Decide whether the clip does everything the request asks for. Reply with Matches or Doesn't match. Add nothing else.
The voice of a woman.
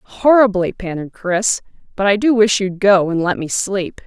Matches